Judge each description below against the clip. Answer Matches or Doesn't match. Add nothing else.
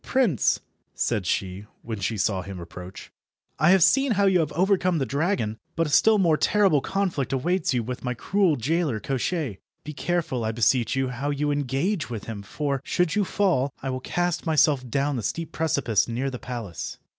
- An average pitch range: Doesn't match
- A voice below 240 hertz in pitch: Matches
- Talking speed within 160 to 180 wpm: Doesn't match